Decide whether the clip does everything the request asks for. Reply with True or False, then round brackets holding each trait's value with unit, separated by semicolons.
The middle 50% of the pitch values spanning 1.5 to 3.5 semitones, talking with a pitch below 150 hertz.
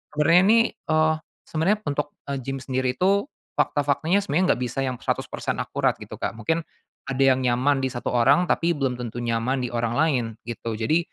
False (4.4 semitones; 135 Hz)